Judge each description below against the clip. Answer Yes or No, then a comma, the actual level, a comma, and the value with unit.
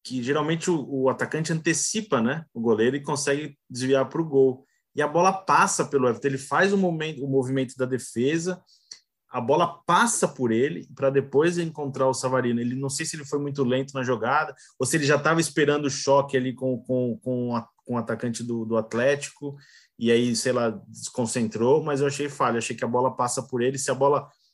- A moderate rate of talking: No, fast, 215 wpm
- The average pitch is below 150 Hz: Yes, low, 135 Hz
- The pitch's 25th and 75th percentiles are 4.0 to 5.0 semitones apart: No, average, 2.9 semitones